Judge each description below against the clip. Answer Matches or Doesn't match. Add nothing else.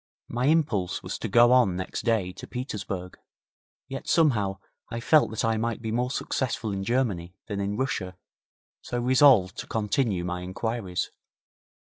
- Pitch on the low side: Matches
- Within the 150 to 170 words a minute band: Matches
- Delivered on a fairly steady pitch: Doesn't match